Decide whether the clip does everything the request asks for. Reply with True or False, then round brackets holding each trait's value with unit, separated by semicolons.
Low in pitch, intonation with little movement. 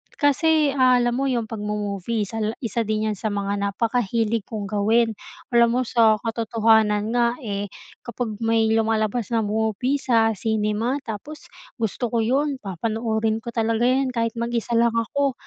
False (225 Hz; 2.0 semitones)